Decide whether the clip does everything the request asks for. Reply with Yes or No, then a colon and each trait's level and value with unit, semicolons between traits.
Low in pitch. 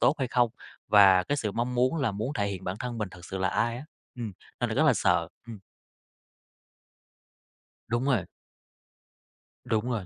Yes: low, 115 Hz